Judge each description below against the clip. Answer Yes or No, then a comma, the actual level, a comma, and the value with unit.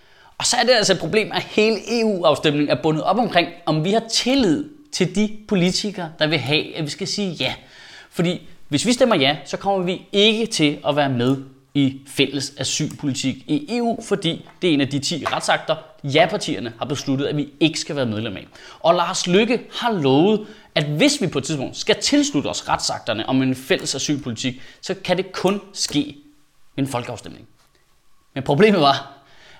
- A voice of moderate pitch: Yes, medium, 160 Hz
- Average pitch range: No, wide, 6.5 semitones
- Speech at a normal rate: Yes, average, 195 wpm